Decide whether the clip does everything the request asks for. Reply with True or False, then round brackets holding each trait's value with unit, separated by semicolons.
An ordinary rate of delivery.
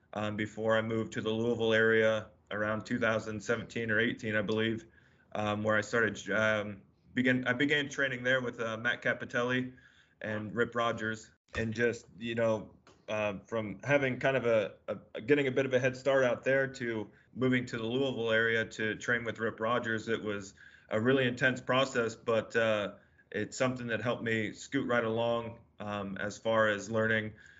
True (180 wpm)